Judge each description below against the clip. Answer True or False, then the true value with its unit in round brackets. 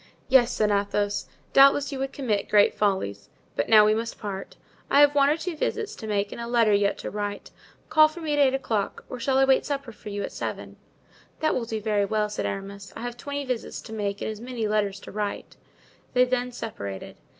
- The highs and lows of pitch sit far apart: False (4.7 semitones)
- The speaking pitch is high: True (225 Hz)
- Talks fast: True (225 wpm)